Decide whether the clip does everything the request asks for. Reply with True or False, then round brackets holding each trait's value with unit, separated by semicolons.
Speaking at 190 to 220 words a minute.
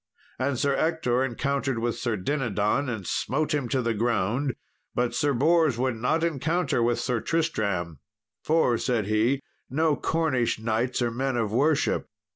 False (155 wpm)